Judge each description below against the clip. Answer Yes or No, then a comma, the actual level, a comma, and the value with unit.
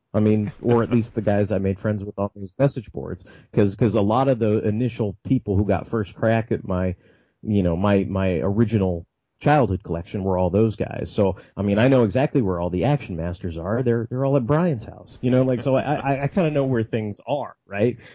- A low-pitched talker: Yes, low, 110 Hz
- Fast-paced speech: Yes, fast, 235 wpm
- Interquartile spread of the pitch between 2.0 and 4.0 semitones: No, average, 4.5 semitones